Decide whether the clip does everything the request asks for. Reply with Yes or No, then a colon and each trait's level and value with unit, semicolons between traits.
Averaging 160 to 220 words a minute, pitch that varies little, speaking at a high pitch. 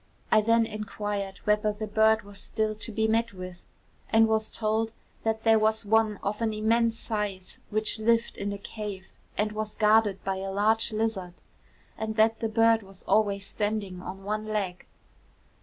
Yes: average, 175 wpm; narrow, 1.6 semitones; high, 215 Hz